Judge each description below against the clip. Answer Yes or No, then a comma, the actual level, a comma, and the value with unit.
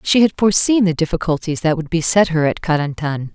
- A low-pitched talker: No, medium, 170 Hz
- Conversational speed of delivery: Yes, average, 195 wpm